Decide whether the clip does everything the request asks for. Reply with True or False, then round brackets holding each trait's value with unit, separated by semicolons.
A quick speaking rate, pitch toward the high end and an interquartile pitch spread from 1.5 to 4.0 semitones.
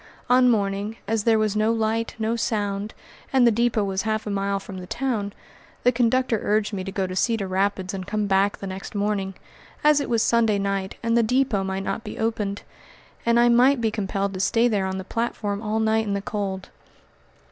True (210 wpm; 210 Hz; 2.6 semitones)